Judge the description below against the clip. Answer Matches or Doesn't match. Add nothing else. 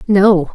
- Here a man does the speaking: Doesn't match